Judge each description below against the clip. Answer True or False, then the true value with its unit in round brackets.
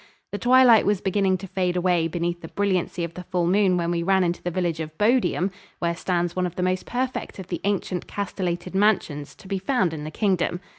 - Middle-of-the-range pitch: True (180 Hz)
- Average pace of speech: False (225 wpm)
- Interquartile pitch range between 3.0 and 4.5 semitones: False (2.4 semitones)